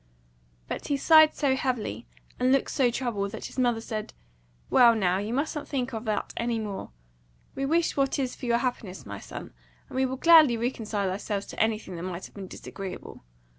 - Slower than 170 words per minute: No, average, 195 wpm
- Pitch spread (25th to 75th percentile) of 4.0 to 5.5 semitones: Yes, average, 4.5 semitones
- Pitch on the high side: Yes, high, 235 Hz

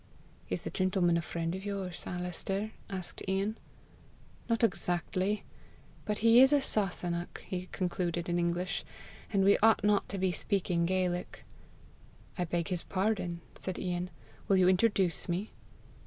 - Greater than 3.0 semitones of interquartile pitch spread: No, narrow, 2.4 semitones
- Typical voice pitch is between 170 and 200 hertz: Yes, medium, 185 Hz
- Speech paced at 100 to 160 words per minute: Yes, average, 145 wpm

